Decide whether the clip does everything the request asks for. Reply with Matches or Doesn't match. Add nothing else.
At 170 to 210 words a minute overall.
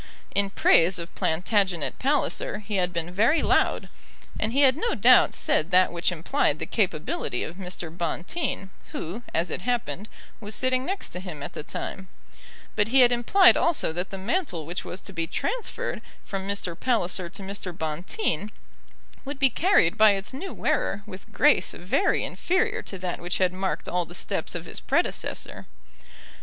Matches